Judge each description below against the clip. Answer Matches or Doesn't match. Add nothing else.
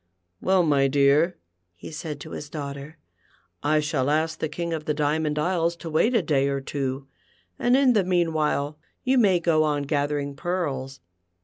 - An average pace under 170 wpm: Doesn't match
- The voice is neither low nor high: Matches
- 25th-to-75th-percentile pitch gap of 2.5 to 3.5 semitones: Matches